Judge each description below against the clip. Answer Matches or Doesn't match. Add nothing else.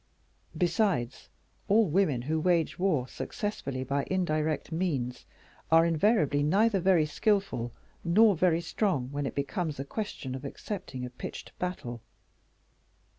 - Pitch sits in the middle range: Matches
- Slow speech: Matches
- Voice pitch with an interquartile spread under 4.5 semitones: Doesn't match